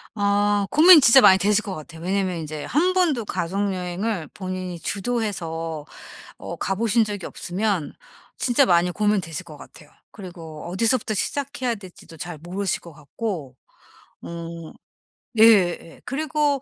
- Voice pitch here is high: Yes, high, 195 Hz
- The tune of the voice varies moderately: Yes, average, 4.8 semitones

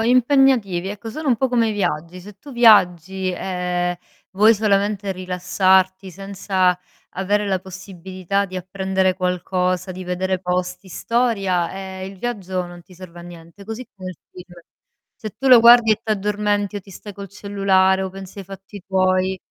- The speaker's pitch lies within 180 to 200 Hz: Yes, high, 190 Hz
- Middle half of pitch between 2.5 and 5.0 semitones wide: No, narrow, 2.1 semitones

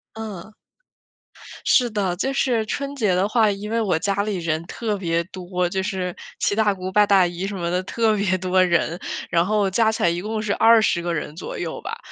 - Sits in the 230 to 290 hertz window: No, high, 195 Hz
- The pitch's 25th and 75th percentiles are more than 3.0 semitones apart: Yes, average, 3.4 semitones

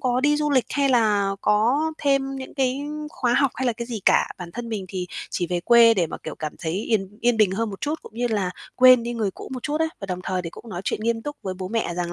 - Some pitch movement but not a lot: Yes, average, 5.0 semitones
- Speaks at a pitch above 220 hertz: Yes, high, 230 Hz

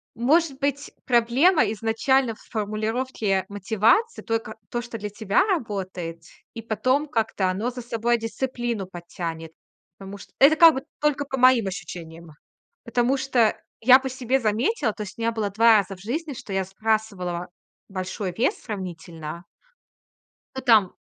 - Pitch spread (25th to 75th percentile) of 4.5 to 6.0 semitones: Yes, average, 4.9 semitones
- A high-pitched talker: Yes, high, 225 Hz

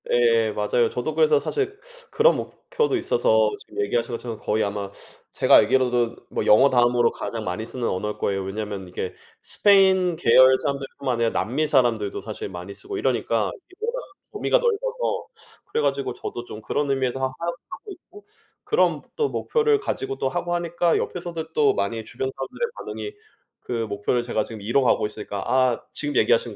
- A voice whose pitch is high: No, low, 130 Hz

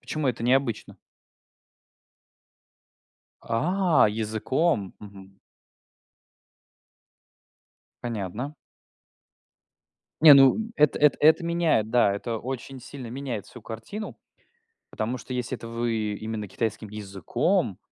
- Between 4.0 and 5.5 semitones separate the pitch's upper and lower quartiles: Yes, average, 4.4 semitones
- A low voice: Yes, low, 120 Hz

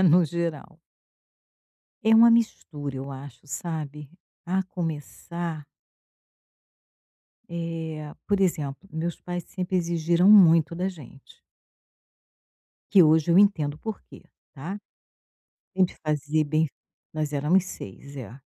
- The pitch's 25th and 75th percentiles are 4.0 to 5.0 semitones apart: No, average, 3.4 semitones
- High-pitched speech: No, medium, 165 Hz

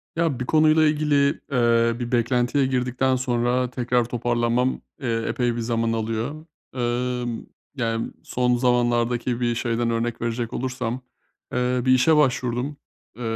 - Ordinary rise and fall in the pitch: No, narrow, 1.5 semitones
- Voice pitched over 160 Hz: No, low, 125 Hz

